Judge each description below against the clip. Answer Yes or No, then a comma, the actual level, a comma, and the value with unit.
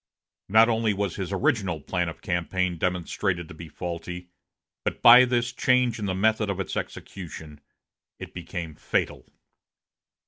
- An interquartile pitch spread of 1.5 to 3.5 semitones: No, average, 4.1 semitones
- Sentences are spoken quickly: No, average, 145 wpm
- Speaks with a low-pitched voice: Yes, very low, 95 Hz